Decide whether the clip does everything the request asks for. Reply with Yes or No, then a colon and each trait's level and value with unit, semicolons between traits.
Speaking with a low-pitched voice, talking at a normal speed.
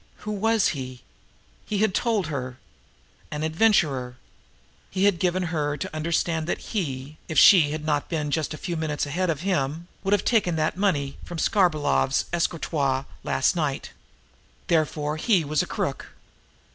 No: medium, 160 Hz; average, 160 wpm